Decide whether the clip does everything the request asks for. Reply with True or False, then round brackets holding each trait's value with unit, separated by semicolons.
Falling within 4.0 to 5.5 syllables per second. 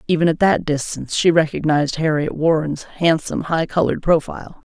False (5.8 syllables/s)